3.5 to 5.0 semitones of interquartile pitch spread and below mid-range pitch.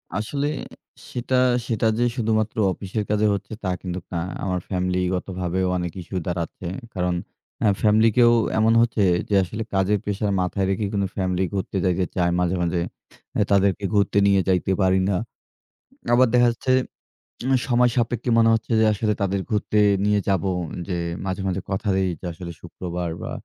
No: average, 3.1 semitones; low, 100 Hz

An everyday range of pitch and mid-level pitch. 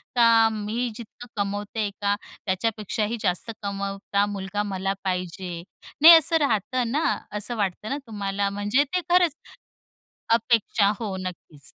No: average, 3.0 semitones; high, 205 Hz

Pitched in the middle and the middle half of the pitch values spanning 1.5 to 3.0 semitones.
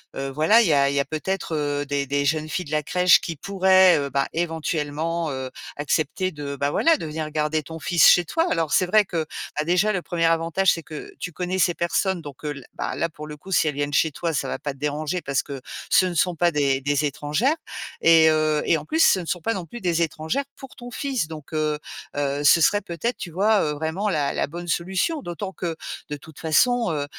No: medium, 160 Hz; average, 3.5 semitones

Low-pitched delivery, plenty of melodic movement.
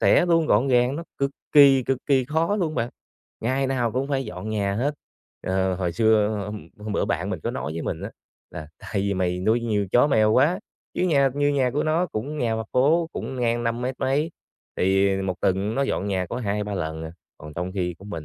Yes: low, 115 Hz; wide, 5.9 semitones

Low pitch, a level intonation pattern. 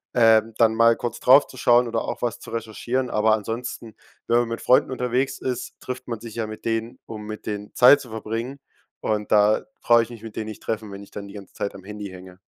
Yes: low, 115 Hz; narrow, 2.1 semitones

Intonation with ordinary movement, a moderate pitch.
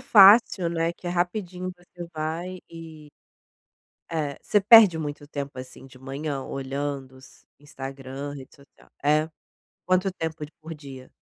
Yes: average, 4.1 semitones; medium, 155 Hz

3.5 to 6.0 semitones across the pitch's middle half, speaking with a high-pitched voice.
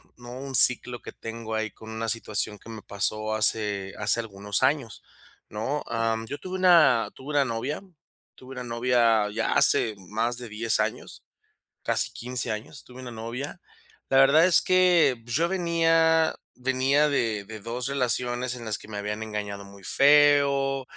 No: average, 4.0 semitones; low, 120 Hz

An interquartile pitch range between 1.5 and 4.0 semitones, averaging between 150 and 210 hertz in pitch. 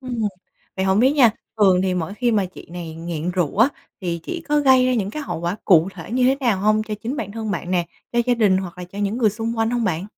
No: average, 4.8 semitones; high, 205 Hz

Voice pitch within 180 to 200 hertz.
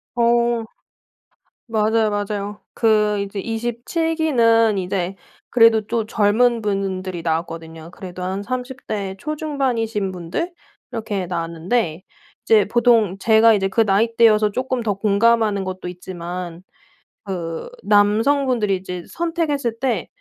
No: high, 215 Hz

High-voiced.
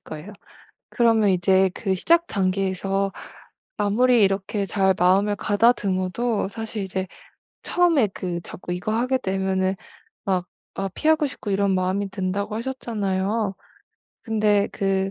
Yes: high, 195 Hz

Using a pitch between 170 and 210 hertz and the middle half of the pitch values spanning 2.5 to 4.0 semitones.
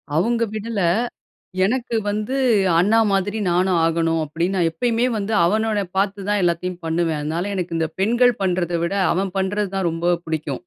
Yes: high, 190 Hz; average, 3.6 semitones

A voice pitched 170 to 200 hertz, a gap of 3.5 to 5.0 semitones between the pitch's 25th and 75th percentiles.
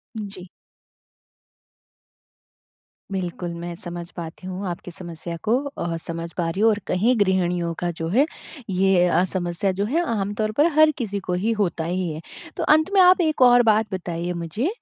Yes: medium, 185 Hz; average, 3.9 semitones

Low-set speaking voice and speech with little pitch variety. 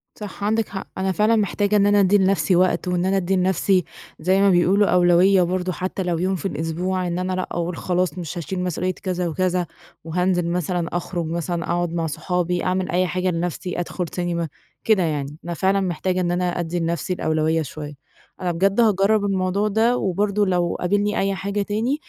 No: medium, 180 Hz; narrow, 2.0 semitones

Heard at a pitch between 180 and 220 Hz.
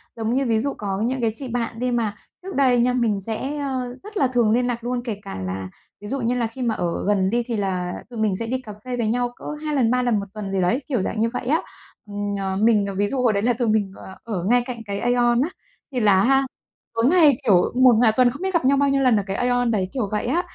No: high, 235 Hz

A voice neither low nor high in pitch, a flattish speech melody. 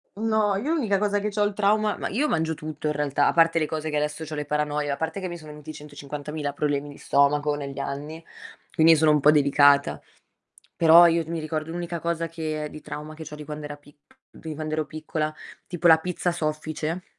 Yes: medium, 155 Hz; narrow, 2.2 semitones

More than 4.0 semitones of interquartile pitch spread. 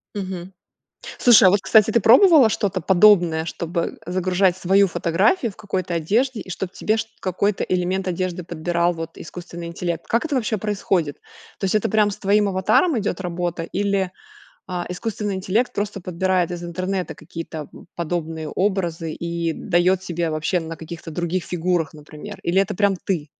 No: average, 2.8 semitones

